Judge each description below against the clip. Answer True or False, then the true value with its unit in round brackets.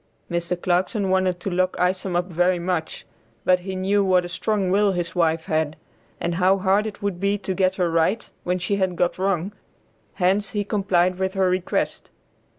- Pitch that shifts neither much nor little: False (1.7 semitones)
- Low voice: False (185 Hz)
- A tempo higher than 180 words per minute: True (190 wpm)